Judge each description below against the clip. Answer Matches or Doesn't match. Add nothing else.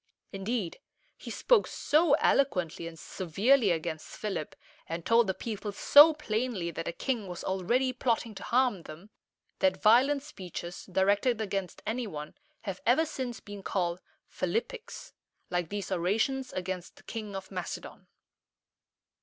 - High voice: Matches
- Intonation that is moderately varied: Doesn't match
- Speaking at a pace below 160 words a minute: Matches